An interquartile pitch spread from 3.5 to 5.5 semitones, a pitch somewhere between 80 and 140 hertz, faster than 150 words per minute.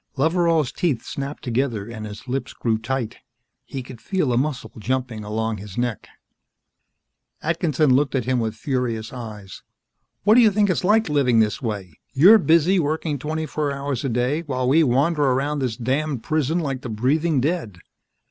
Yes: average, 4.9 semitones; low, 135 Hz; average, 175 wpm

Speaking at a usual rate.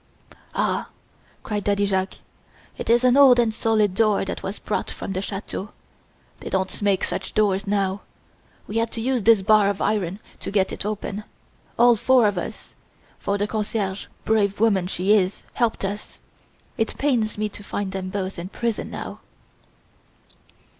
Yes: average, 165 wpm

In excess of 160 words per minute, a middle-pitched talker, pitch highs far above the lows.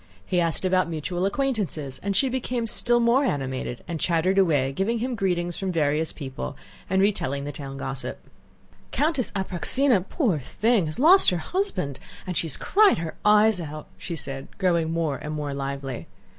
Yes: average, 170 wpm; medium, 175 Hz; wide, 6.9 semitones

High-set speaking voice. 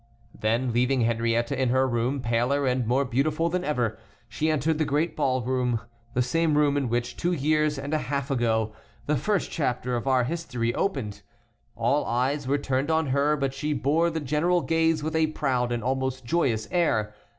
No: low, 135 Hz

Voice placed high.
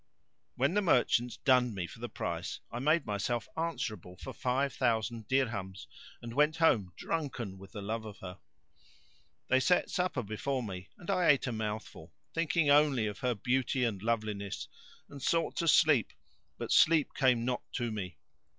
No: low, 120 Hz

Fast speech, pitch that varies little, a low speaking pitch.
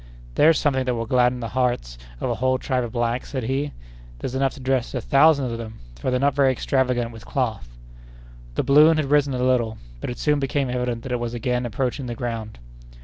Yes: fast, 220 wpm; narrow, 2.3 semitones; low, 125 Hz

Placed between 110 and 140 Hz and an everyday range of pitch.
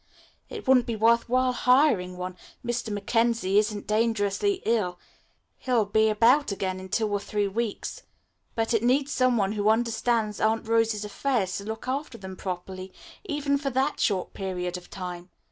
No: high, 220 Hz; average, 3.6 semitones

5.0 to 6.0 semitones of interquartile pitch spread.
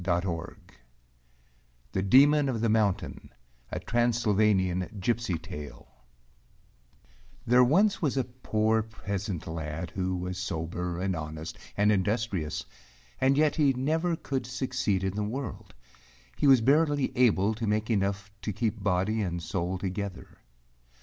Yes: average, 5.3 semitones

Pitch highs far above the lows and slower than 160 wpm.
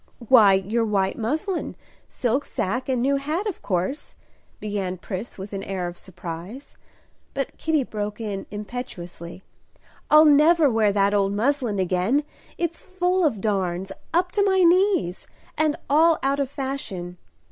Yes: wide, 7.5 semitones; average, 145 wpm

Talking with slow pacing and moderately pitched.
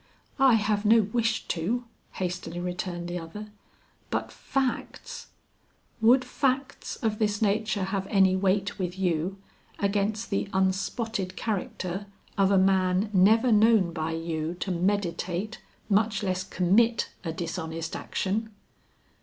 No: slow, 130 wpm; high, 195 Hz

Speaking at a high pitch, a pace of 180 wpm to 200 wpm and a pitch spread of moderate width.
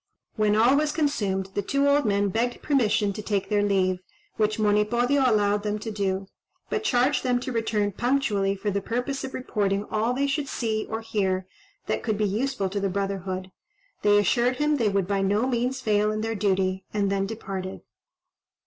Yes: high, 210 Hz; average, 190 wpm; average, 3.7 semitones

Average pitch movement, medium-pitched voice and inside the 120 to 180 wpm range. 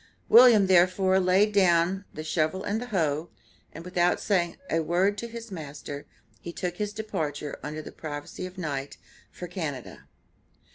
Yes: average, 4.2 semitones; medium, 180 Hz; average, 160 wpm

